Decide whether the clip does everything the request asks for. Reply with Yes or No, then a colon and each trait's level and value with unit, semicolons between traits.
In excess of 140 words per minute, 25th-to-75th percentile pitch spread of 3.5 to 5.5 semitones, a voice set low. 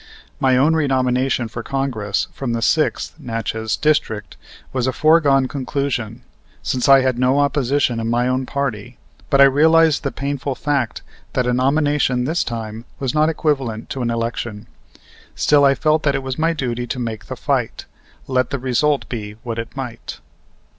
No: average, 170 wpm; average, 3.1 semitones; low, 130 Hz